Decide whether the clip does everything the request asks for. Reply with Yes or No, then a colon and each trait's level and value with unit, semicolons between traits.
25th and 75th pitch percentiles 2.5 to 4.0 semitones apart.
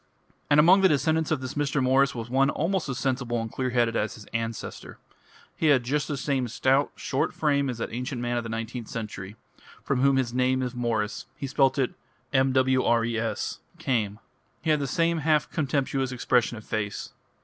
Yes: average, 3.1 semitones